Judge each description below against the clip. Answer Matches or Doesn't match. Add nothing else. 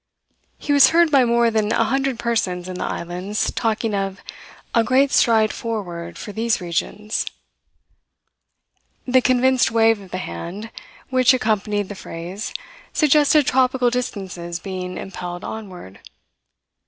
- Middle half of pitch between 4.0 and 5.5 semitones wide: Matches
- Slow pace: Matches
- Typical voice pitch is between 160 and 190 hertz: Doesn't match